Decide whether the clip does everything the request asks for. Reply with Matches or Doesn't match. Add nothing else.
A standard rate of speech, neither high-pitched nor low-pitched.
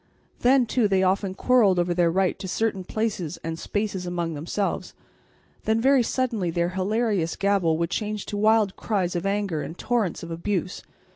Doesn't match